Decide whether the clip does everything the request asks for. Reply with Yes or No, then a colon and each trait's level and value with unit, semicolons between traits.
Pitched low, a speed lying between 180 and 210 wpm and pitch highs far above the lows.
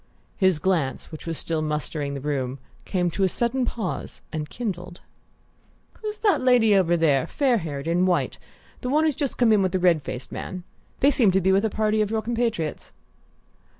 No: medium, 185 Hz; average, 195 wpm; wide, 6.3 semitones